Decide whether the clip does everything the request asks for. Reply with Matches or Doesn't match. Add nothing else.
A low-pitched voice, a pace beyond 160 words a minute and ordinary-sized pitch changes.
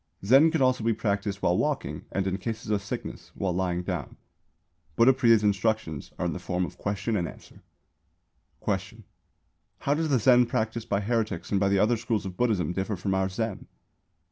Matches